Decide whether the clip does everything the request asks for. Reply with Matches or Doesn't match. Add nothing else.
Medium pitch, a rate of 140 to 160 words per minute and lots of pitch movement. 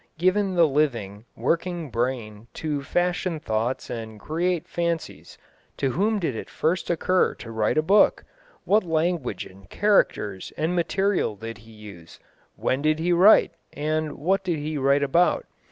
Matches